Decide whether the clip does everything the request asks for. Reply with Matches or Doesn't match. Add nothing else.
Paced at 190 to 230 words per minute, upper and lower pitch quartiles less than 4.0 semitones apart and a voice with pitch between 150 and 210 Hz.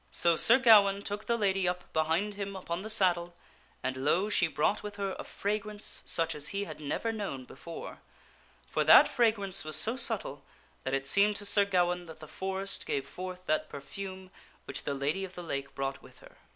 Doesn't match